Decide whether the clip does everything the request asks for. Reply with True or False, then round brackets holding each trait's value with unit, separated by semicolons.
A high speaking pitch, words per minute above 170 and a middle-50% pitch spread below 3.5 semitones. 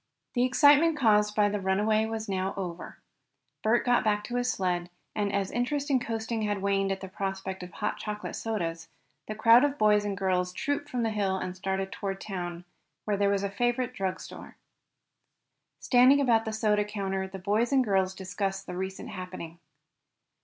True (205 Hz; 180 wpm; 2.9 semitones)